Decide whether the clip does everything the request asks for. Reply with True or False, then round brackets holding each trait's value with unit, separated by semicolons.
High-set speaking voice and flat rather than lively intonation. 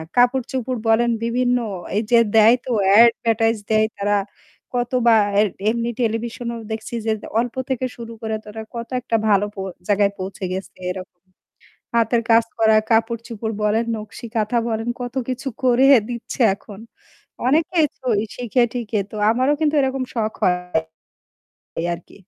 True (230 Hz; 2.1 semitones)